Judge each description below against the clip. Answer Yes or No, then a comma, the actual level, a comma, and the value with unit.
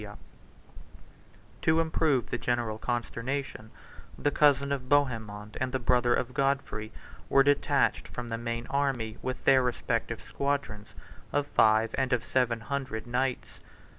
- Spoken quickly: No, slow, 135 wpm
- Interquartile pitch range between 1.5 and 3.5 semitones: Yes, average, 3.1 semitones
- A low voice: Yes, low, 125 Hz